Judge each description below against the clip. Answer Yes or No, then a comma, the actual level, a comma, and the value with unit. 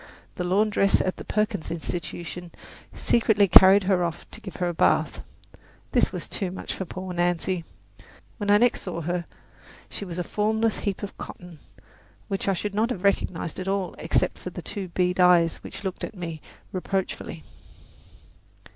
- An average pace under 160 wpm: No, average, 175 wpm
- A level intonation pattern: Yes, narrow, 2.3 semitones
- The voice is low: No, medium, 185 Hz